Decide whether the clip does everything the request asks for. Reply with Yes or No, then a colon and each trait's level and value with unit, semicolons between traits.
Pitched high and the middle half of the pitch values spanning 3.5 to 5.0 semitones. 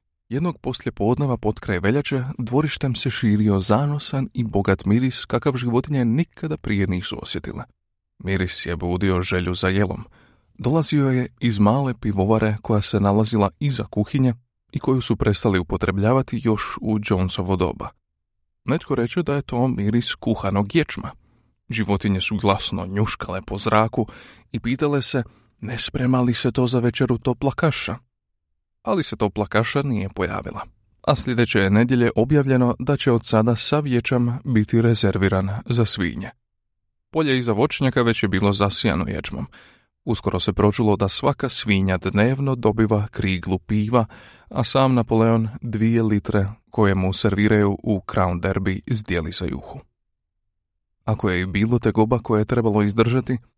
No: low, 110 Hz; average, 4.0 semitones